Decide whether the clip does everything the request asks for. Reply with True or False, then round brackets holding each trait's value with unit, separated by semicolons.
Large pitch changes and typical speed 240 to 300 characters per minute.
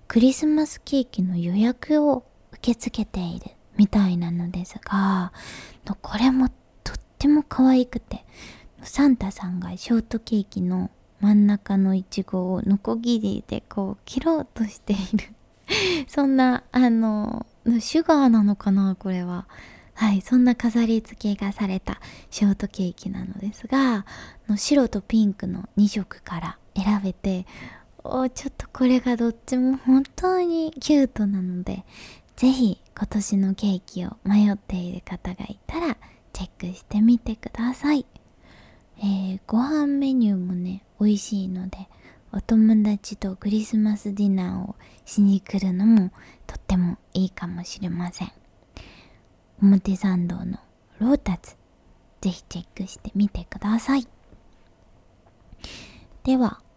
False (4.0 semitones; 270 characters per minute)